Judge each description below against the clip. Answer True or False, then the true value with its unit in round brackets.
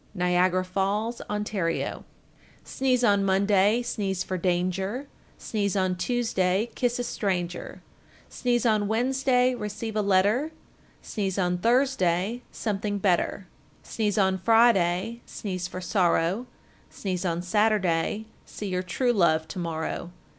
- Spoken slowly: True (125 wpm)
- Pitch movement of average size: True (3.8 semitones)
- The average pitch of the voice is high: True (200 Hz)